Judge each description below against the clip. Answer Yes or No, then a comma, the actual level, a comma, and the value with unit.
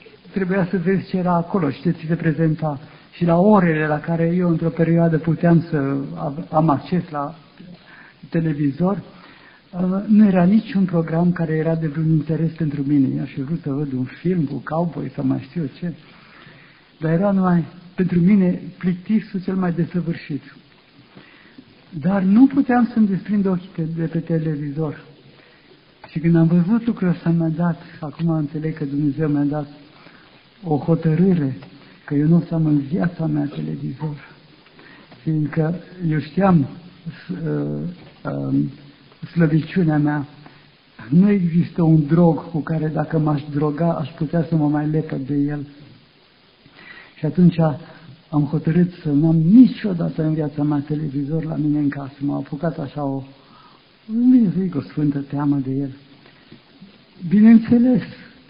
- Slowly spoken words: No, average, 150 wpm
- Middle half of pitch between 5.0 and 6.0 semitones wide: No, average, 3.0 semitones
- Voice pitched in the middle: Yes, medium, 160 Hz